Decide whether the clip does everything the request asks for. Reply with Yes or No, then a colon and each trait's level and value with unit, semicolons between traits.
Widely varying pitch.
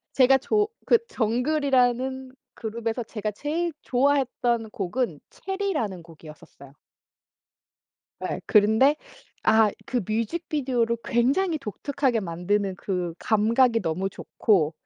No: average, 4.6 semitones